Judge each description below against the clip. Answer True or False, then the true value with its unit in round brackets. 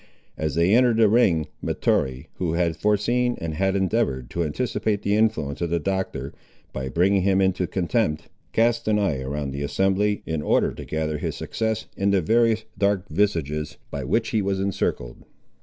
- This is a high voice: False (95 Hz)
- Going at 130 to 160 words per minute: False (175 wpm)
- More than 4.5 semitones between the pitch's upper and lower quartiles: True (5.3 semitones)